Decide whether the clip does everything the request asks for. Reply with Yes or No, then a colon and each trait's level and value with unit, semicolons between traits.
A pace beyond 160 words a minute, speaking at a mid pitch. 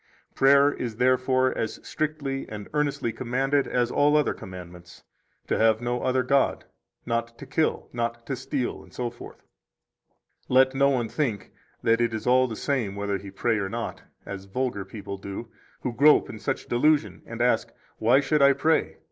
No: average, 175 wpm; low, 125 Hz